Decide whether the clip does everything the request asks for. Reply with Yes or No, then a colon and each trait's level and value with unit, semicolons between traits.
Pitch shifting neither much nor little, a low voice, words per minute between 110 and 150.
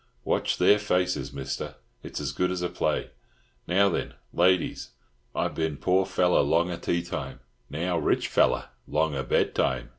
Yes: average, 3.3 semitones; very low, 85 Hz; average, 145 wpm